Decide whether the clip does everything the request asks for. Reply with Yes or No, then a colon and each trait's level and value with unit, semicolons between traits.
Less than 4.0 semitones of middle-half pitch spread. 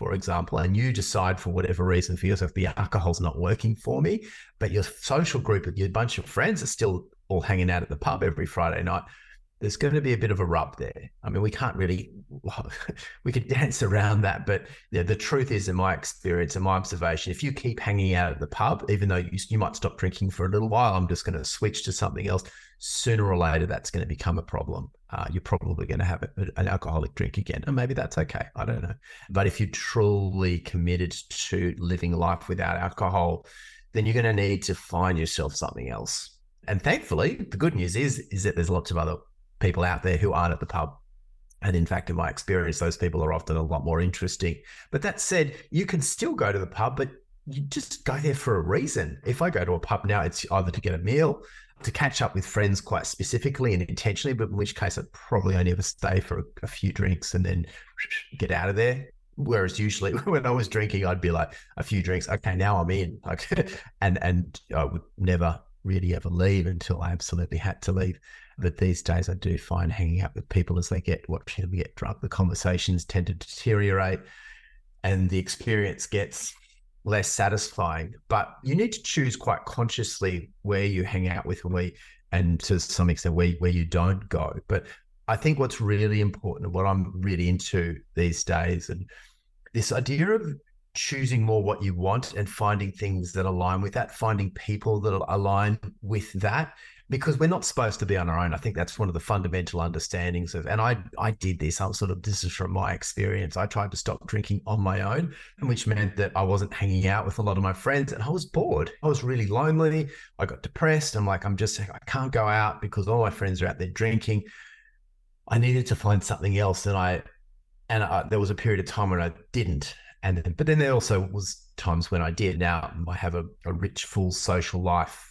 Yes: average, 3.5 semitones